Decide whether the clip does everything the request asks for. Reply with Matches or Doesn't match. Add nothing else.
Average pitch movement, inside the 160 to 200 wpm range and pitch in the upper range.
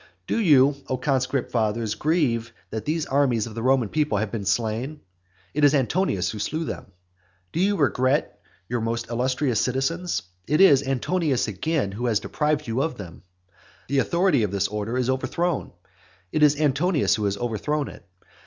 Doesn't match